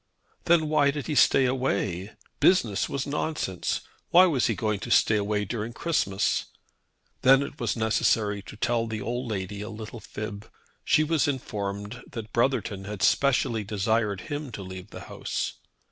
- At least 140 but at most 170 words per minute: Yes, average, 160 wpm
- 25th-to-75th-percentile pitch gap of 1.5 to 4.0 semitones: No, average, 4.7 semitones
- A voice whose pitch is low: Yes, low, 115 Hz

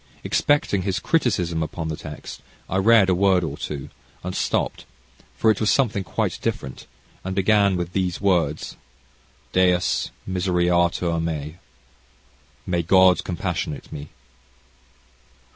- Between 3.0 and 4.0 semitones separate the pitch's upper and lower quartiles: No, narrow, 2.5 semitones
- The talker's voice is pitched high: No, very low, 90 Hz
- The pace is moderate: No, slow, 125 wpm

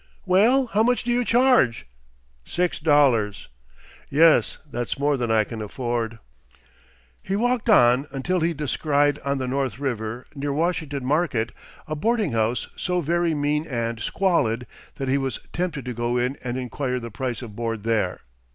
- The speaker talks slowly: No, average, 160 wpm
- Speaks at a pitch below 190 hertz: Yes, medium, 140 Hz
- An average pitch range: No, wide, 6.1 semitones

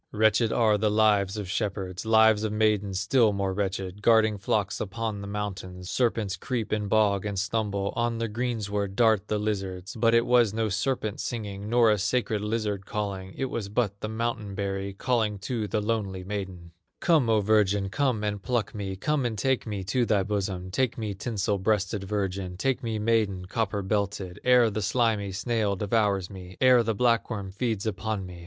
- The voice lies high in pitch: No, low, 105 Hz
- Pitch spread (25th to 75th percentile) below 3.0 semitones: Yes, narrow, 2.4 semitones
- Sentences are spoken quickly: No, average, 185 wpm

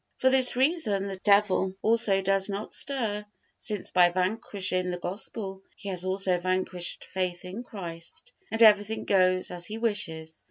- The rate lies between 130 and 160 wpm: Yes, average, 155 wpm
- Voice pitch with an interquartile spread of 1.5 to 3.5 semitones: Yes, average, 2.9 semitones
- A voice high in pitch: Yes, high, 195 Hz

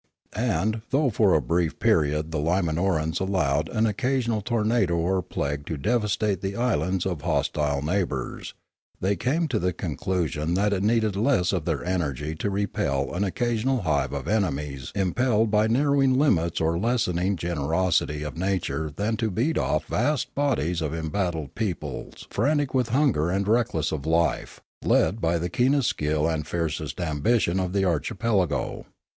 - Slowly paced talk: No, average, 160 wpm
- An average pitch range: No, wide, 5.8 semitones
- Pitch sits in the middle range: No, very low, 95 Hz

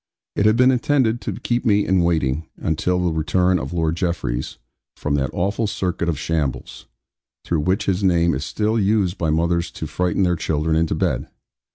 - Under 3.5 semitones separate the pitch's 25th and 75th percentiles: No, average, 3.8 semitones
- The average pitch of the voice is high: No, very low, 85 Hz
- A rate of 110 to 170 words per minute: No, average, 185 wpm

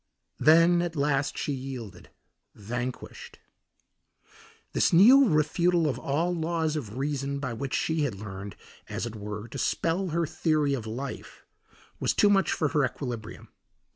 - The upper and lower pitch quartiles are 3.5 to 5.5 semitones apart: Yes, average, 5.2 semitones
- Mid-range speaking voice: Yes, medium, 145 Hz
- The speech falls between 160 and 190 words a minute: No, average, 145 wpm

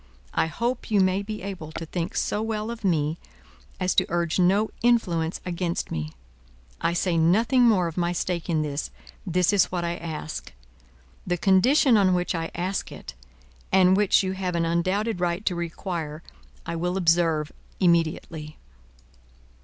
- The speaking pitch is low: No, medium, 180 Hz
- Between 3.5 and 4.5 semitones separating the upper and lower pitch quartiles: No, average, 2.8 semitones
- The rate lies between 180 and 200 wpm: No, average, 160 wpm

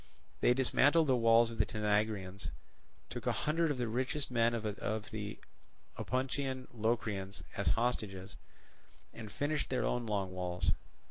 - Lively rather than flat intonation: No, average, 3.6 semitones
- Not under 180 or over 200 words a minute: No, average, 140 wpm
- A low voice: Yes, low, 115 Hz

